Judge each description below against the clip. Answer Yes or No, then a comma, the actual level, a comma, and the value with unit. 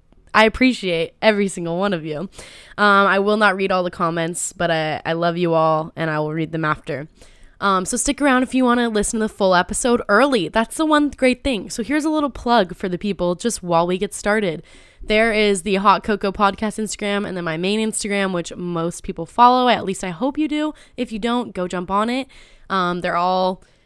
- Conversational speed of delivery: No, fast, 230 wpm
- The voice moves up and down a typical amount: Yes, average, 4.8 semitones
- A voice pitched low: No, high, 200 Hz